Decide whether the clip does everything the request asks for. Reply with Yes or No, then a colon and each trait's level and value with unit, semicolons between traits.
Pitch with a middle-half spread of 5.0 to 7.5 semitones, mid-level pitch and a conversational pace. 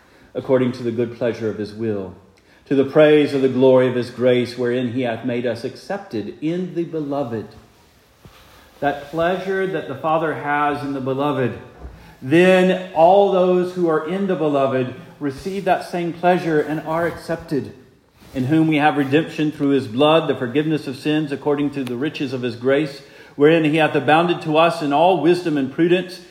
No: average, 4.3 semitones; medium, 145 Hz; average, 180 wpm